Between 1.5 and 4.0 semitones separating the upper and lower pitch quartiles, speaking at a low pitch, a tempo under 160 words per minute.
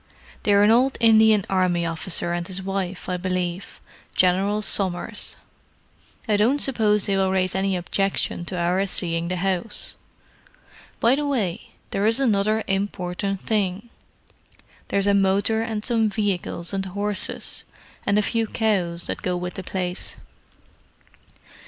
No: average, 2.7 semitones; high, 195 Hz; average, 140 wpm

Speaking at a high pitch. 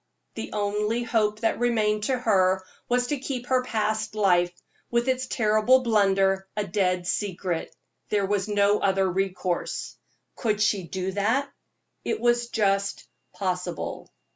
Yes: high, 210 Hz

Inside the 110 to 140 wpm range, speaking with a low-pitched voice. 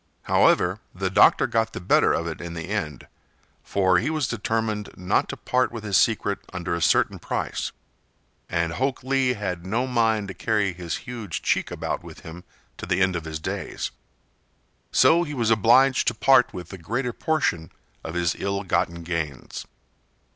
No: average, 175 wpm; low, 100 Hz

